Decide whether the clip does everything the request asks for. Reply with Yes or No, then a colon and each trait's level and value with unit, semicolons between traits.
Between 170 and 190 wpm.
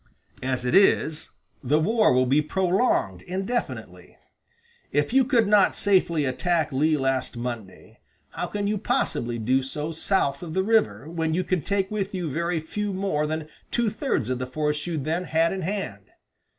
Yes: average, 175 wpm